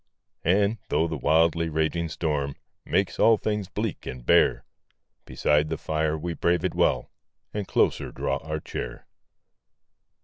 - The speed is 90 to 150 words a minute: Yes, average, 140 wpm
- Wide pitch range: No, average, 3.1 semitones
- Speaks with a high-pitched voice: No, very low, 80 Hz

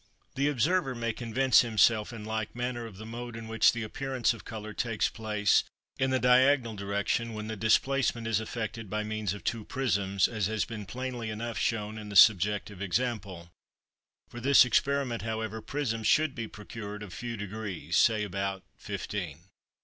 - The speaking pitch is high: No, low, 110 Hz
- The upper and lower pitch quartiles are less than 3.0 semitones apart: Yes, narrow, 2.5 semitones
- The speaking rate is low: No, average, 170 wpm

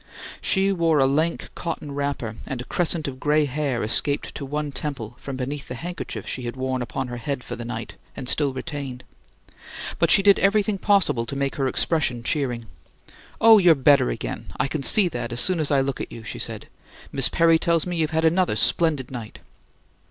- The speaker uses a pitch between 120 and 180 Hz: Yes, medium, 140 Hz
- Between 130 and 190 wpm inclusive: No, fast, 205 wpm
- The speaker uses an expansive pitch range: No, average, 4.3 semitones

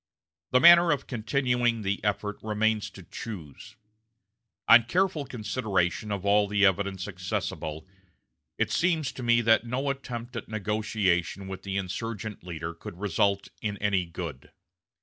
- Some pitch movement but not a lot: Yes, average, 3.7 semitones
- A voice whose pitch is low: Yes, low, 105 Hz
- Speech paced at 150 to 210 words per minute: No, average, 140 wpm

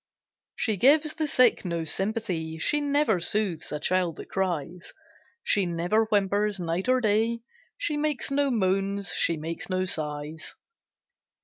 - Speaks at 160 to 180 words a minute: No, average, 140 wpm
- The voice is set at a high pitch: Yes, high, 195 Hz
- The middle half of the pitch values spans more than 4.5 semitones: Yes, wide, 5.4 semitones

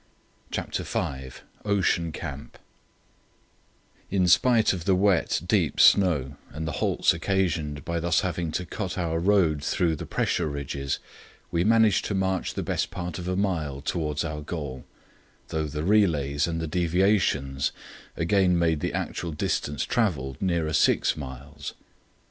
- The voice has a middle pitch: No, very low, 85 Hz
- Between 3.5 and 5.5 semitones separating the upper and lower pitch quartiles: Yes, average, 4.0 semitones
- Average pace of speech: Yes, average, 145 wpm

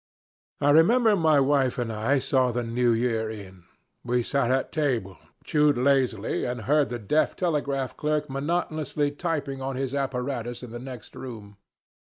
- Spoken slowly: No, average, 160 wpm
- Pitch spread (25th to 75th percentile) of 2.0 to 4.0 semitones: Yes, average, 3.4 semitones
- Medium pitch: No, low, 130 Hz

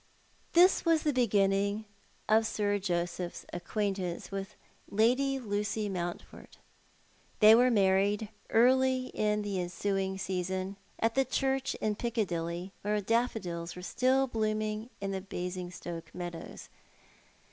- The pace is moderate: No, slow, 115 wpm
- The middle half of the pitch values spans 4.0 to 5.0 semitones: No, average, 3.5 semitones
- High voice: Yes, high, 205 Hz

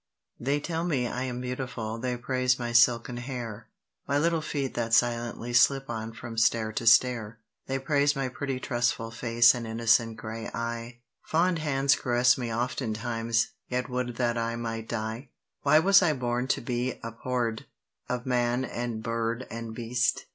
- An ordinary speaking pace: Yes, average, 165 wpm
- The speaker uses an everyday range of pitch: No, narrow, 1.9 semitones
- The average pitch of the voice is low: Yes, low, 120 Hz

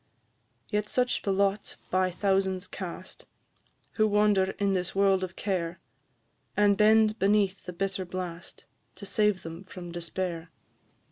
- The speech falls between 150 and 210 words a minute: No, slow, 135 wpm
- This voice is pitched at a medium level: No, high, 195 Hz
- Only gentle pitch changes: Yes, narrow, 2.1 semitones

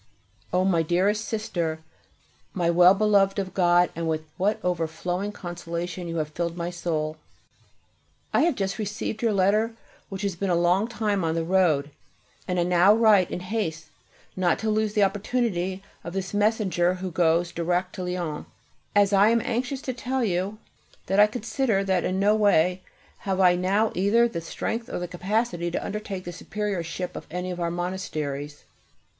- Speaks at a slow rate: No, average, 175 wpm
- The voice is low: No, medium, 185 Hz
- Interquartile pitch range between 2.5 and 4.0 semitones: Yes, average, 3.3 semitones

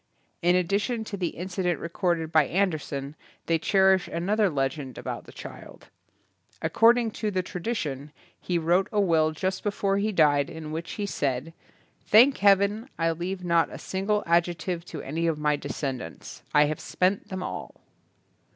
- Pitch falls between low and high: Yes, medium, 175 Hz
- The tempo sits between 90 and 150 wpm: No, average, 170 wpm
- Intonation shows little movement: No, average, 4.0 semitones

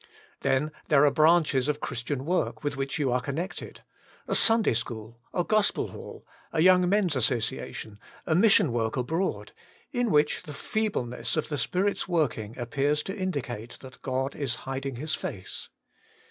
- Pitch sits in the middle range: Yes, medium, 145 Hz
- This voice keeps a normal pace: Yes, average, 165 wpm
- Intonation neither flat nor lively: No, wide, 5.7 semitones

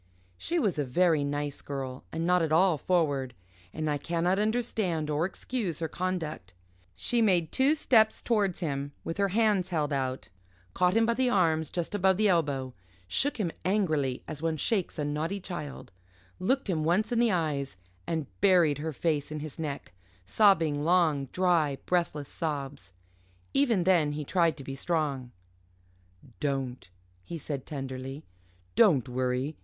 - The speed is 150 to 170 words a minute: Yes, average, 160 wpm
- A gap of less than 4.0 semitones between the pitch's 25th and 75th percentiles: No, average, 4.7 semitones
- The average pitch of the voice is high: No, medium, 160 Hz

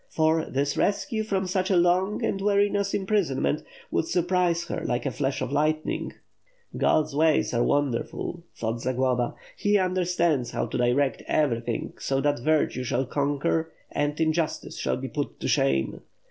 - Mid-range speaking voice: Yes, medium, 155 Hz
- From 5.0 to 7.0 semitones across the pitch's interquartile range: Yes, average, 5.3 semitones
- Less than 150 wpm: No, average, 160 wpm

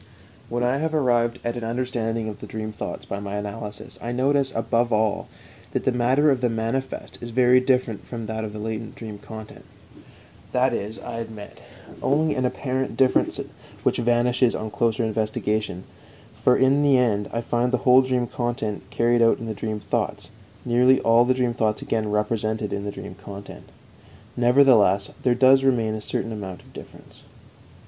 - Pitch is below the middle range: Yes, low, 115 Hz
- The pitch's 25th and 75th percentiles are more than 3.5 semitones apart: No, average, 2.7 semitones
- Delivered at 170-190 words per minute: Yes, average, 180 wpm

